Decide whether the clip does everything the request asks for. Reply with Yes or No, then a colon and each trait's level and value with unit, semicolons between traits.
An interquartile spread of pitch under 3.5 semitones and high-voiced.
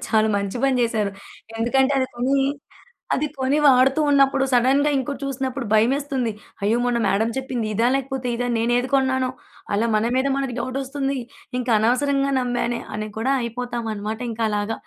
Yes: average, 2.9 semitones; very high, 250 Hz